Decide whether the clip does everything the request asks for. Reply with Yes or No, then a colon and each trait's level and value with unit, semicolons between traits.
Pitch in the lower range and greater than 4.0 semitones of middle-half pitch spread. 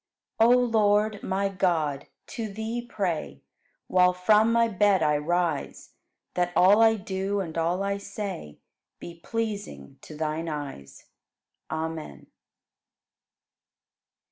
No: high, 190 Hz; average, 4.7 semitones